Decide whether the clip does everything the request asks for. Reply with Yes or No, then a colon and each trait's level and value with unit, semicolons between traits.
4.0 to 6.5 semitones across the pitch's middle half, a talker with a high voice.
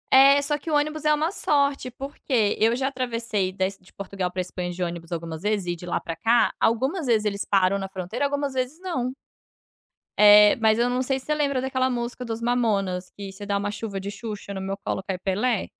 Yes: average, 5.2 semitones; high, 225 Hz